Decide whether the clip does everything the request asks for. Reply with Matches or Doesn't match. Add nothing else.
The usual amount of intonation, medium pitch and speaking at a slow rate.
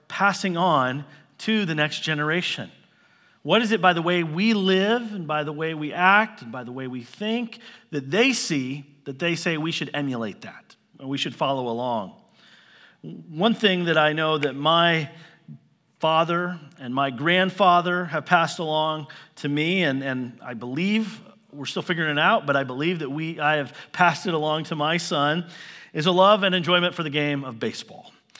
Doesn't match